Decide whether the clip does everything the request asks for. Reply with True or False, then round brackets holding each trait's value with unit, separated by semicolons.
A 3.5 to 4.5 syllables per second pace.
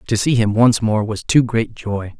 True (4.4 syllables/s)